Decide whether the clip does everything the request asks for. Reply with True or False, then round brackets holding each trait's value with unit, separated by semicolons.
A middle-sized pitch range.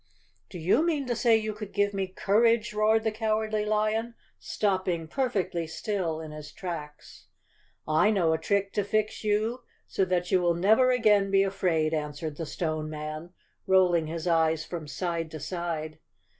True (4.9 semitones)